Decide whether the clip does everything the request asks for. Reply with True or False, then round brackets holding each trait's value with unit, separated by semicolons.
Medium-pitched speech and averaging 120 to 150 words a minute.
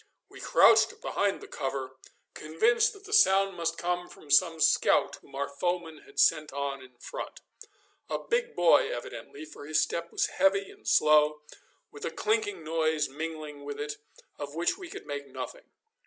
False (160 Hz; 170 wpm)